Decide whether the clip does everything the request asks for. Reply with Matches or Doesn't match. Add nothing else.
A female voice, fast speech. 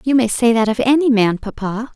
Matches